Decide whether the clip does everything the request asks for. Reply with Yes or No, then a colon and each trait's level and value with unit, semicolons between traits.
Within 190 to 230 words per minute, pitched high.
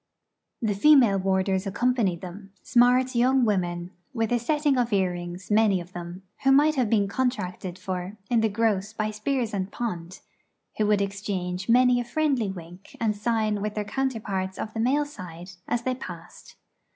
No: average, 170 wpm; high, 210 Hz